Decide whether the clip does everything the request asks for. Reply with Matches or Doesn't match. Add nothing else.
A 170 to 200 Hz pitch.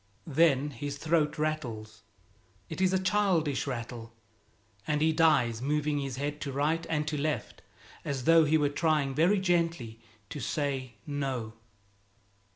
Doesn't match